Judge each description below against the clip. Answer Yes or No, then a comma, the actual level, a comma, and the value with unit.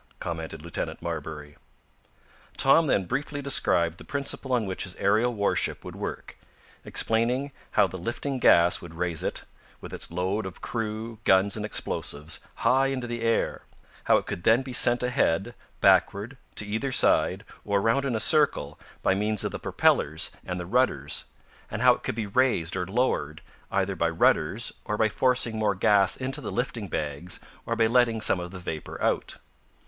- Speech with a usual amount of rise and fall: No, wide, 5.7 semitones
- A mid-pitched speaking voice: No, low, 105 Hz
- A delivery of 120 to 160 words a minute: No, average, 175 wpm